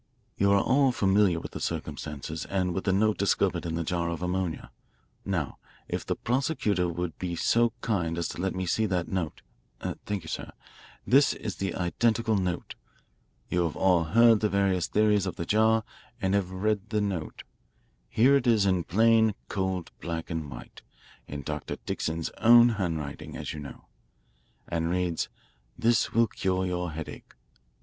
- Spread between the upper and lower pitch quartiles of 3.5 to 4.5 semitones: Yes, average, 4.1 semitones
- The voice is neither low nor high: No, very low, 95 Hz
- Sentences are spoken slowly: No, average, 170 wpm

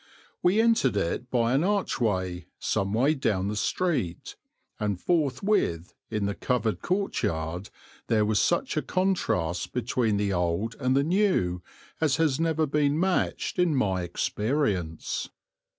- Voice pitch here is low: Yes, low, 120 Hz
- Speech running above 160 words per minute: No, slow, 135 wpm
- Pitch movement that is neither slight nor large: No, wide, 8.6 semitones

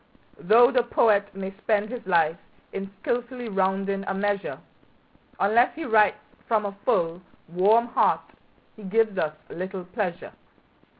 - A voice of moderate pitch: No, high, 200 Hz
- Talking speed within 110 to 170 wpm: Yes, slow, 135 wpm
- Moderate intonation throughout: Yes, average, 3.1 semitones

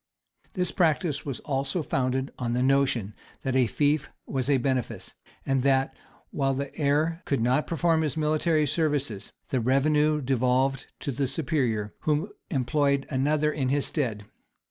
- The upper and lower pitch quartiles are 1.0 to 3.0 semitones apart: Yes, average, 2.7 semitones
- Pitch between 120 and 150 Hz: Yes, medium, 140 Hz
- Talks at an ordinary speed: Yes, average, 150 wpm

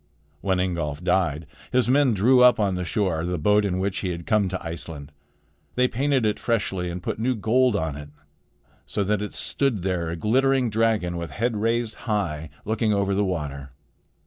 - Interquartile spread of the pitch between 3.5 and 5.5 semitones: Yes, average, 4.8 semitones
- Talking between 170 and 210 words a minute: Yes, average, 190 wpm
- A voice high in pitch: No, low, 100 Hz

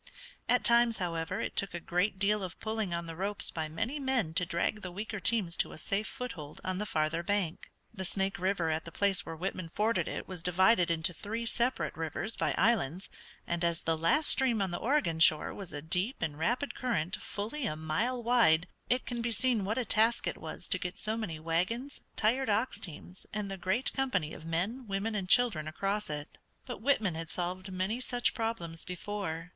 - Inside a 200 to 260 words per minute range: Yes, fast, 205 wpm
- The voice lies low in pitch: No, high, 195 Hz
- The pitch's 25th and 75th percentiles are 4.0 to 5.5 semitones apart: Yes, average, 5.2 semitones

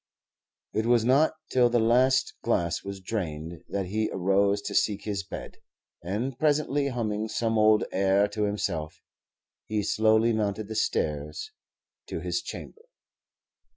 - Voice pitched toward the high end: No, low, 110 Hz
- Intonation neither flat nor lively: Yes, average, 3.3 semitones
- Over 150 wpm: No, average, 140 wpm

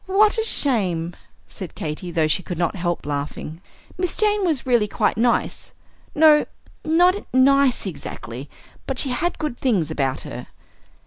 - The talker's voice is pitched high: Yes, high, 235 Hz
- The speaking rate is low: No, average, 150 wpm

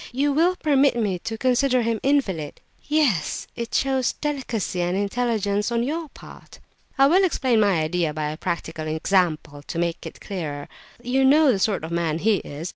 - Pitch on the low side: No, high, 220 Hz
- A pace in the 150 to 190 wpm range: Yes, average, 185 wpm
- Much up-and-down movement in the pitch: Yes, wide, 7.8 semitones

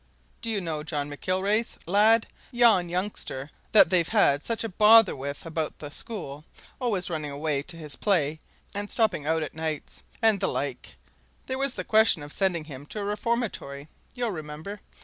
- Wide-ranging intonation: Yes, wide, 6.2 semitones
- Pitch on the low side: No, medium, 180 Hz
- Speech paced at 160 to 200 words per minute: Yes, average, 175 wpm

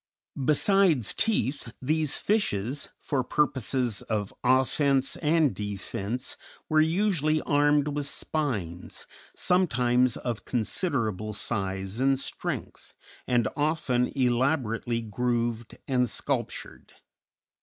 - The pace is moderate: No, slow, 90 wpm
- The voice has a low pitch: Yes, low, 130 Hz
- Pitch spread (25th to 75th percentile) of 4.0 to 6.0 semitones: Yes, average, 4.4 semitones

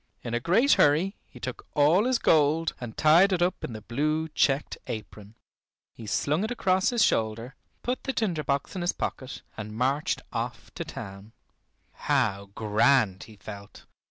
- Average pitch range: No, wide, 7.8 semitones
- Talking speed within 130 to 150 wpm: No, average, 170 wpm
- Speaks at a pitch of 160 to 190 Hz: No, medium, 140 Hz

